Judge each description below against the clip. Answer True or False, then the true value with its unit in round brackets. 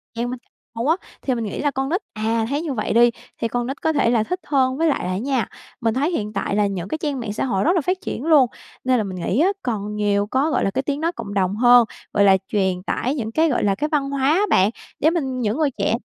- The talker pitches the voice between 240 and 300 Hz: True (245 Hz)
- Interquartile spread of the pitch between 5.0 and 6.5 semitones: True (5.4 semitones)